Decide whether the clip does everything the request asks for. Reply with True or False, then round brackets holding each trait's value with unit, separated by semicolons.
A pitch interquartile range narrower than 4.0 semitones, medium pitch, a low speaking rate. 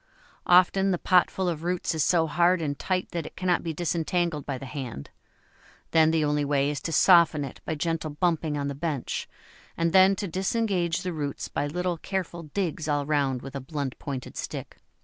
False (3.5 semitones; 160 Hz; 195 wpm)